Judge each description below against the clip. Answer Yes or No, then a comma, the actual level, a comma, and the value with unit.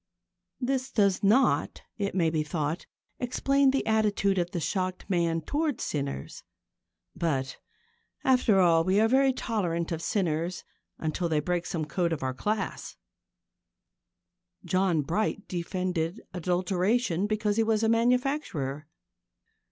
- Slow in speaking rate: Yes, slow, 130 wpm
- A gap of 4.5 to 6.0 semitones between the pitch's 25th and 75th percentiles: Yes, average, 5.1 semitones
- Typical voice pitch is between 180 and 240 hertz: Yes, medium, 185 Hz